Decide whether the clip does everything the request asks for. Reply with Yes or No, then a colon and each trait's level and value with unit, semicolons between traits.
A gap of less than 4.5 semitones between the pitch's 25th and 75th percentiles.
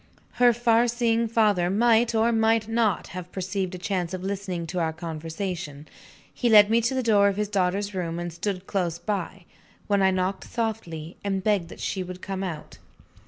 Yes: average, 3.8 semitones